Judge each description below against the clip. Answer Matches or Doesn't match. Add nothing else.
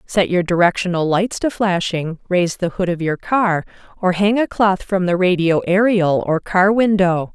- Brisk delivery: Doesn't match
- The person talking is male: Doesn't match